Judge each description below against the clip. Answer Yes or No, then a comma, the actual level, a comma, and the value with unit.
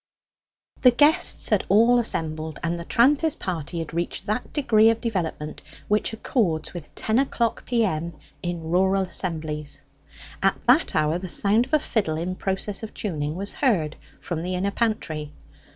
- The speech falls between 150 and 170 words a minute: Yes, average, 160 wpm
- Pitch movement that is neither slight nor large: No, wide, 5.7 semitones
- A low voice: No, medium, 185 Hz